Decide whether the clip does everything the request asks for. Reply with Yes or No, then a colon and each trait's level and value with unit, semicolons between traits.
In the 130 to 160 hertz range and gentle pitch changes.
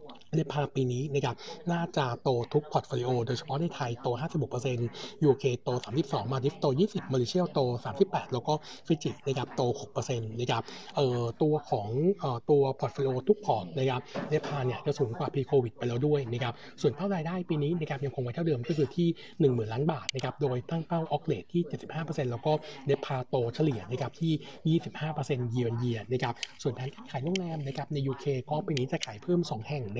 No: medium, 140 Hz; average, 3.7 semitones